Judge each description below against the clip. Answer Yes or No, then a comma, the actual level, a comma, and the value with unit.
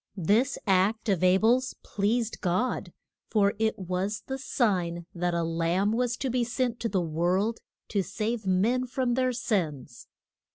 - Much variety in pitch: No, average, 4.8 semitones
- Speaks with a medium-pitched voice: No, high, 210 Hz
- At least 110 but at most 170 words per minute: Yes, average, 160 wpm